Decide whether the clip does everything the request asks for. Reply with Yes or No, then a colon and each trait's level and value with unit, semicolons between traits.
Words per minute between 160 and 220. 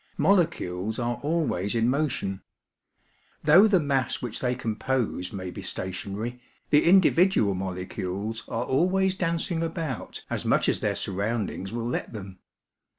No: average, 140 wpm